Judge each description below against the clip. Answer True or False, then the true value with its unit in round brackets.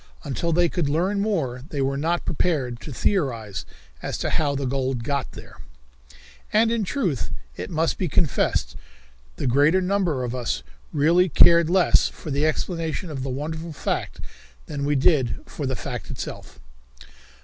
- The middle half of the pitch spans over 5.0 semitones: False (4.5 semitones)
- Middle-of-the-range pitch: True (150 Hz)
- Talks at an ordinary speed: True (160 wpm)